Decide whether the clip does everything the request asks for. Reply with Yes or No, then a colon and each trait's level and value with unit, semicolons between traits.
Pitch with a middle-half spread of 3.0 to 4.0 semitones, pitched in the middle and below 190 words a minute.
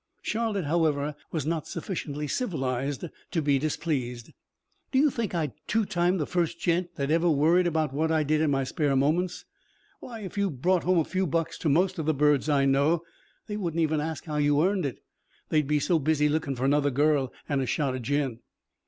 No: average, 3.4 semitones; medium, 155 Hz; fast, 205 wpm